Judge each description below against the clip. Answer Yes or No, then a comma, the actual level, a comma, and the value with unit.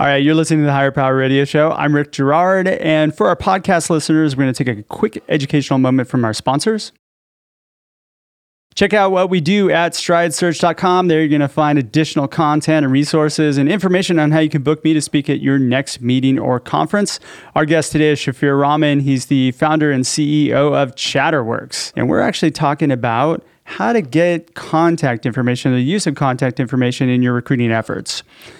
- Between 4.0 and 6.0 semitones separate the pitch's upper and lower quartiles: No, average, 3.2 semitones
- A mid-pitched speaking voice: Yes, medium, 150 Hz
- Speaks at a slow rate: No, average, 195 wpm